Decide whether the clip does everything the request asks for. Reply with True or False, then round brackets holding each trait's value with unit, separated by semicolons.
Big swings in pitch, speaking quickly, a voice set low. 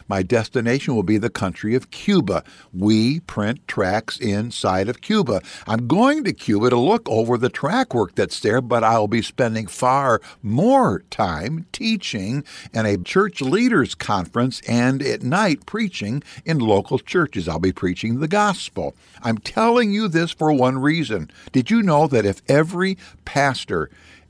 False (6.8 semitones; 160 wpm; 125 Hz)